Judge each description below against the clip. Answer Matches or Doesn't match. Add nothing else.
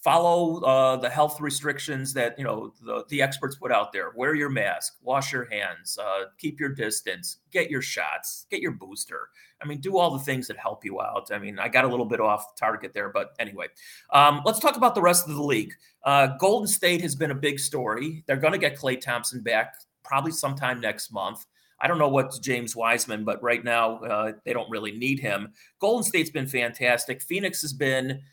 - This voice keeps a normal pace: Doesn't match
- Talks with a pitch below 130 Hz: Doesn't match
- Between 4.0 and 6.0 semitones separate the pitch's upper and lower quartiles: Matches